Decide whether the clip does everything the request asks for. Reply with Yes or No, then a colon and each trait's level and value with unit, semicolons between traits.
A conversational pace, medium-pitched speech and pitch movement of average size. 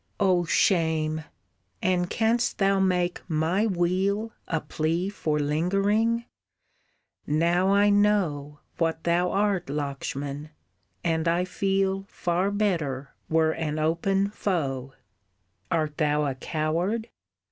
No: slow, 110 wpm; medium, 175 Hz; average, 4.1 semitones